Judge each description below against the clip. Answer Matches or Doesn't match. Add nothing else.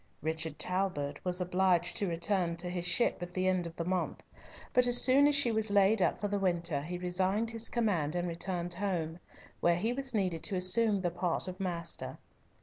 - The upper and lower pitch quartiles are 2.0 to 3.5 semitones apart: Matches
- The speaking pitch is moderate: Matches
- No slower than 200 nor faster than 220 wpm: Matches